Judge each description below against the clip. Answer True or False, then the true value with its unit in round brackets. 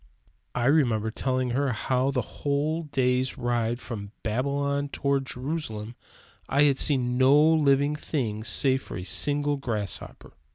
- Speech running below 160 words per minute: True (140 wpm)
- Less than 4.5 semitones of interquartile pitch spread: True (3.0 semitones)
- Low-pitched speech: True (130 Hz)